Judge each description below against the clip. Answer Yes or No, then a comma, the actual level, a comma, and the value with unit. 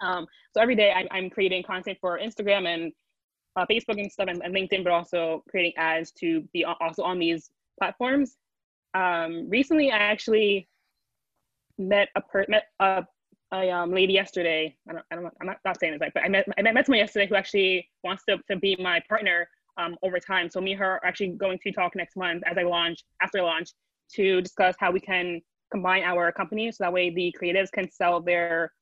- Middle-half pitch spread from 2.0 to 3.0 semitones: Yes, narrow, 2.5 semitones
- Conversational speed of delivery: No, fast, 210 wpm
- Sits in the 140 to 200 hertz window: Yes, medium, 185 Hz